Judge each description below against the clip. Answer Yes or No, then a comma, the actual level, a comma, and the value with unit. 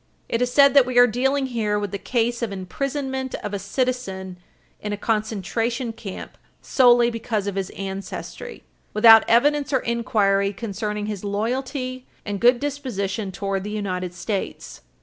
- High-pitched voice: Yes, high, 225 Hz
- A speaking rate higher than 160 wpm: No, average, 155 wpm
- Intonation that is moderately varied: Yes, average, 4.1 semitones